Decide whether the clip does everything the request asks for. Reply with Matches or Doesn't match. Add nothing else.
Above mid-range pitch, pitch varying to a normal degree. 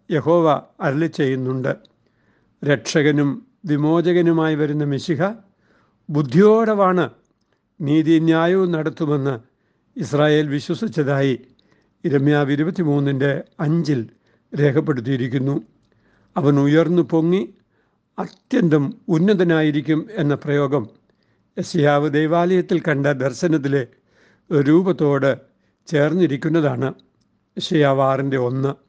Doesn't match